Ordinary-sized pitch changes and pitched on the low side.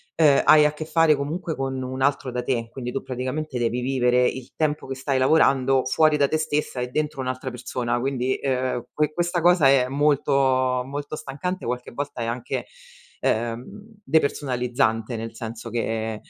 Yes: average, 3.2 semitones; low, 130 Hz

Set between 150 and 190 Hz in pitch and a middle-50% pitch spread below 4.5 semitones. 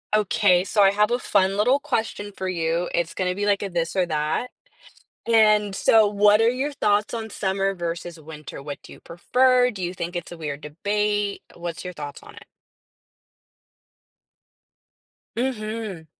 No: high, 200 Hz; average, 3.7 semitones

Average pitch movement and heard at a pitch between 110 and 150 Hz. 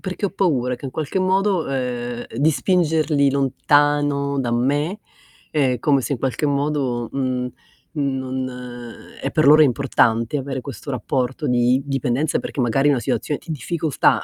Yes: average, 3.0 semitones; medium, 140 Hz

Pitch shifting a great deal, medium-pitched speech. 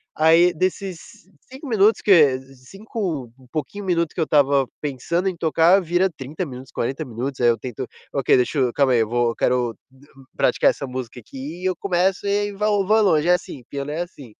Yes: wide, 6.2 semitones; medium, 155 Hz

